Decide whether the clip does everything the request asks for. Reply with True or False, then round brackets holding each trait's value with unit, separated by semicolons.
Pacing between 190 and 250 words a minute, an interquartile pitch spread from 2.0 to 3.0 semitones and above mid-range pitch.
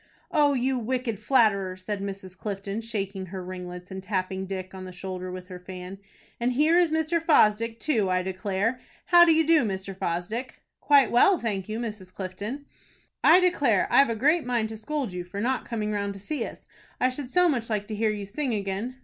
False (205 wpm; 5.3 semitones; 215 Hz)